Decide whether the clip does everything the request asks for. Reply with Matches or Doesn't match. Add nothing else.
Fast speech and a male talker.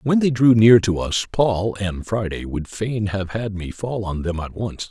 Matches